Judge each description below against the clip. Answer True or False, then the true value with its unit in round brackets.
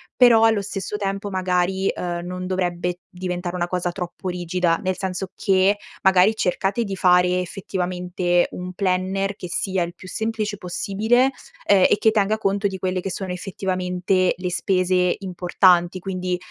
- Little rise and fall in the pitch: True (1.5 semitones)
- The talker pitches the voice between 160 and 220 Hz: True (185 Hz)